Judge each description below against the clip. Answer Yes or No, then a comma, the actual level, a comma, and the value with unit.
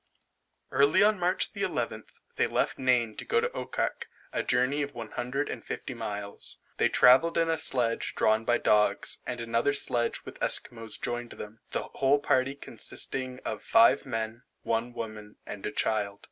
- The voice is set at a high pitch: No, low, 120 Hz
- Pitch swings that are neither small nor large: Yes, average, 3.9 semitones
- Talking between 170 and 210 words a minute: No, average, 160 wpm